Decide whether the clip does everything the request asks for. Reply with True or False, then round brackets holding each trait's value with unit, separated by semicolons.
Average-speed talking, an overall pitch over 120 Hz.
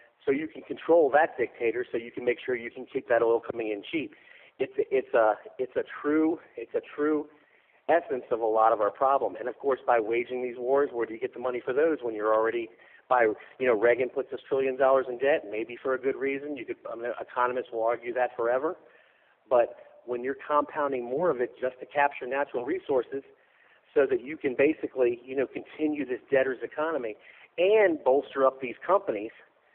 False (215 wpm; 140 Hz)